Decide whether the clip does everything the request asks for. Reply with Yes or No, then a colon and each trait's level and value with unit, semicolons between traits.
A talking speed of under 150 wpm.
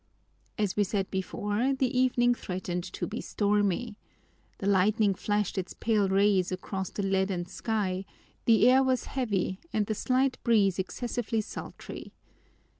Yes: average, 140 wpm